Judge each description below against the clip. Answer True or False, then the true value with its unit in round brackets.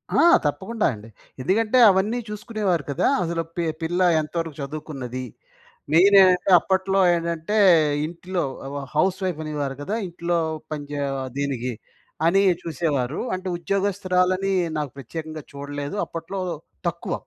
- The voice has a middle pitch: True (170 Hz)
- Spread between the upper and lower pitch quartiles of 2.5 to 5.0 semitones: True (4.5 semitones)